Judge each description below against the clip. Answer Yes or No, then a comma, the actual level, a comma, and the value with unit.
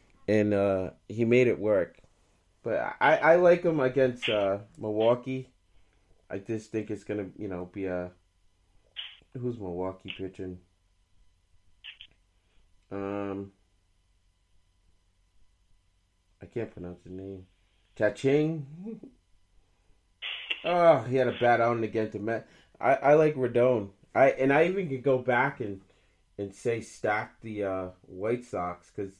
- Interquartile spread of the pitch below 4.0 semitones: No, average, 4.6 semitones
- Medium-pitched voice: No, low, 100 Hz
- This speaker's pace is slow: Yes, slow, 125 wpm